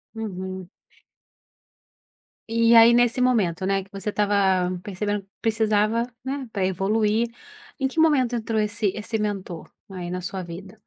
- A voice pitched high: Yes, high, 210 Hz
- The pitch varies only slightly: No, average, 3.3 semitones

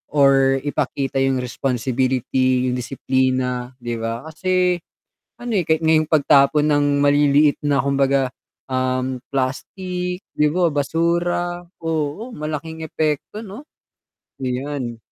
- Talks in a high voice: No, medium, 145 Hz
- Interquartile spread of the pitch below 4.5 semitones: Yes, average, 3.7 semitones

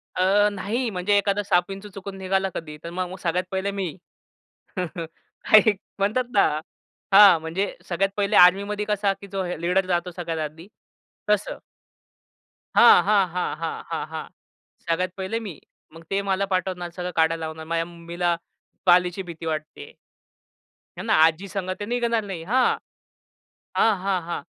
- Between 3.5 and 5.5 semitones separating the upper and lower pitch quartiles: No, average, 2.8 semitones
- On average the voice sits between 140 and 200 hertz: Yes, medium, 185 Hz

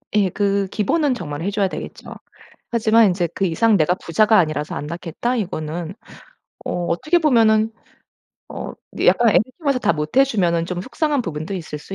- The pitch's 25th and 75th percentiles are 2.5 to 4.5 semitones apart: No, average, 5.2 semitones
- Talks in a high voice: Yes, high, 195 Hz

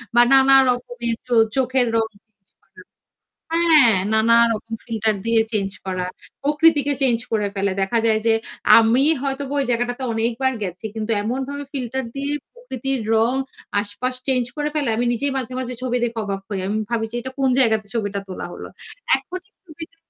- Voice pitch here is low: No, high, 240 Hz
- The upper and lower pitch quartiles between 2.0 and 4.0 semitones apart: Yes, average, 3.4 semitones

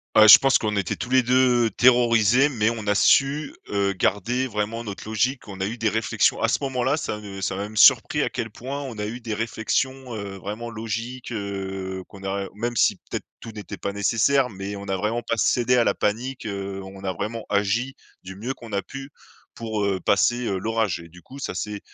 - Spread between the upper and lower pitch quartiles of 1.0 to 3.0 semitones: No, average, 3.5 semitones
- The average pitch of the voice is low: Yes, low, 110 Hz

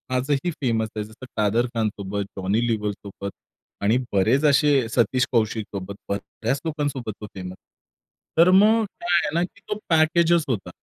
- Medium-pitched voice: No, low, 120 Hz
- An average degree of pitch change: No, wide, 6.4 semitones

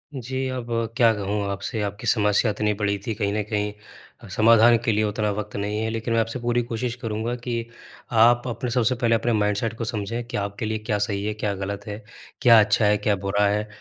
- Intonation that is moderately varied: No, narrow, 2.1 semitones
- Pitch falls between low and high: No, low, 110 Hz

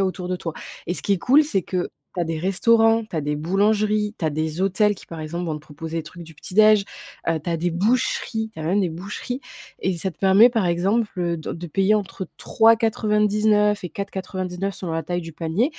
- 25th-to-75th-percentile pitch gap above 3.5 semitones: Yes, average, 4.1 semitones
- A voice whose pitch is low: No, high, 190 Hz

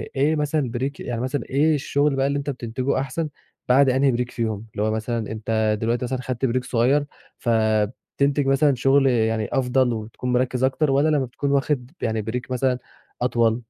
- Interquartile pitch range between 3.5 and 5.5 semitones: No, average, 3.1 semitones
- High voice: No, low, 125 Hz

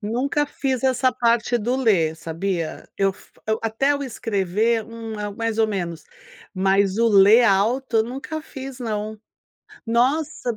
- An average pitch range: Yes, average, 4.0 semitones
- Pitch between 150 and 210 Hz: No, high, 225 Hz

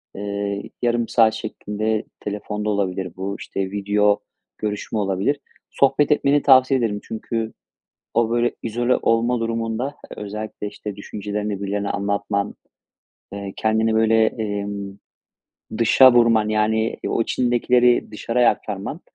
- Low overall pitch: Yes, low, 110 Hz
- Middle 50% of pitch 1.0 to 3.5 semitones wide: Yes, narrow, 2.4 semitones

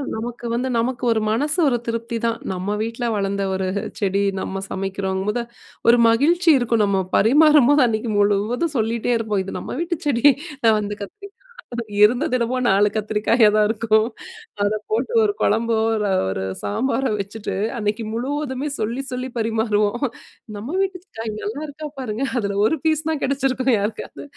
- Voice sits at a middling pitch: No, high, 230 Hz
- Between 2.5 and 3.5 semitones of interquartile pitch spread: No, average, 4.0 semitones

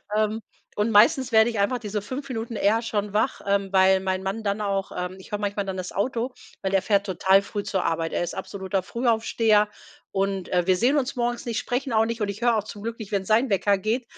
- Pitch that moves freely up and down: No, average, 2.9 semitones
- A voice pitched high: Yes, high, 210 Hz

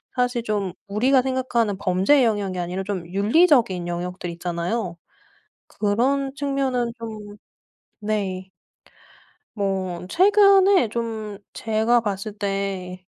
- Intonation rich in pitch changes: No, average, 4.7 semitones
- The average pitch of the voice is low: No, high, 210 Hz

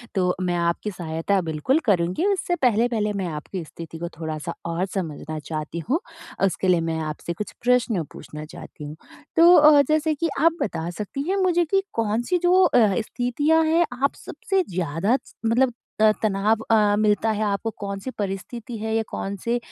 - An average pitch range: No, wide, 7.3 semitones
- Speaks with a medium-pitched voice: No, high, 210 Hz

